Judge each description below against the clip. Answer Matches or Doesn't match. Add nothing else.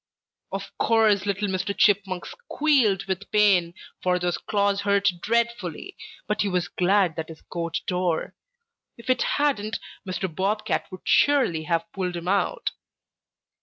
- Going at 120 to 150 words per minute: Matches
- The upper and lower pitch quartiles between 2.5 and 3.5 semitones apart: Matches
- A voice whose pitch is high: Matches